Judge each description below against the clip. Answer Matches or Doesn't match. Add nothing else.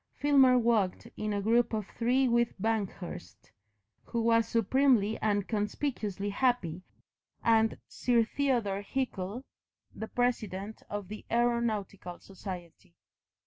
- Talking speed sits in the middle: Doesn't match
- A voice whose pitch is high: Matches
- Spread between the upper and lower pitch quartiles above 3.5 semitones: Doesn't match